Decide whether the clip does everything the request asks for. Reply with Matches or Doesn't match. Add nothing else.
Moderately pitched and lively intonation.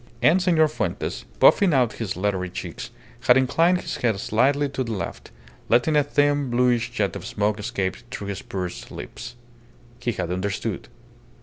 Doesn't match